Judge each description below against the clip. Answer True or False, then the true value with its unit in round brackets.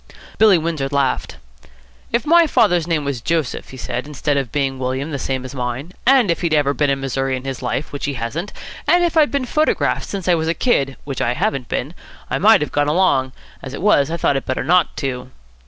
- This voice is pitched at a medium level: True (145 Hz)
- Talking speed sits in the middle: False (230 wpm)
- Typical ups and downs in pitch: True (4.8 semitones)